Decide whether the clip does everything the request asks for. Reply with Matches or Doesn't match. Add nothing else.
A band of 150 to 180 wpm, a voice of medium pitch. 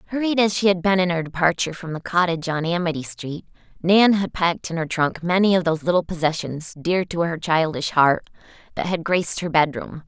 Doesn't match